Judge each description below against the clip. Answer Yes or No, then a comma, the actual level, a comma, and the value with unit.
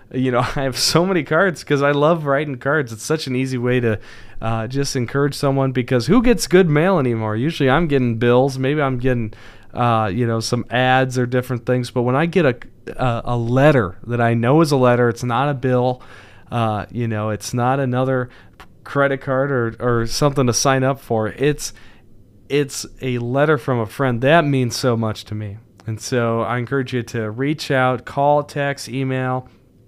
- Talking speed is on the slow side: No, average, 200 wpm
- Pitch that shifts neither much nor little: Yes, average, 3.1 semitones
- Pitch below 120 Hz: No, low, 125 Hz